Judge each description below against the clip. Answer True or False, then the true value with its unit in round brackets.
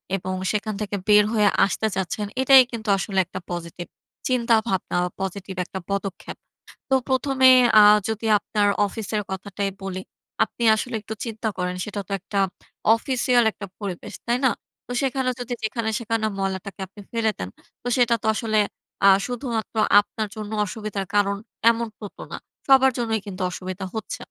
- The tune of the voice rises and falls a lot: False (3.1 semitones)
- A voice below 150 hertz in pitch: False (215 Hz)